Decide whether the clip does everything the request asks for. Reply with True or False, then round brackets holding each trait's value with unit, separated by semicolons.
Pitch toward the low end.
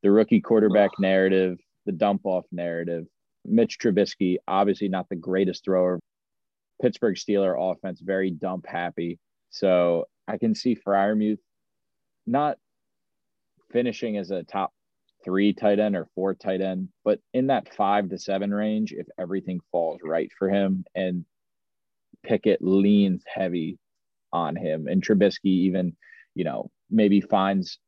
True (95 Hz)